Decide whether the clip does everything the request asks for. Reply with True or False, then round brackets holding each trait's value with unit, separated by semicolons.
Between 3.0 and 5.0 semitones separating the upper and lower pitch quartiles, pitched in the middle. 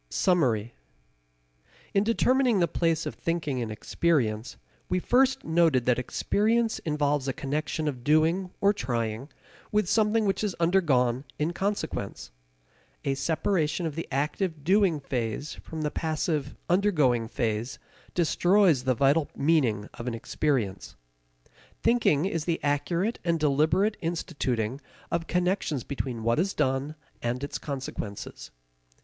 False (5.6 semitones; 155 Hz)